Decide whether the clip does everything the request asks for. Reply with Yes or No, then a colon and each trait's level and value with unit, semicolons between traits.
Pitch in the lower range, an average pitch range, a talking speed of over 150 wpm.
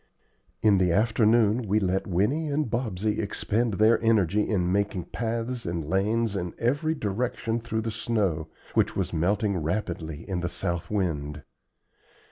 No: low, 105 Hz; average, 4.2 semitones; average, 145 wpm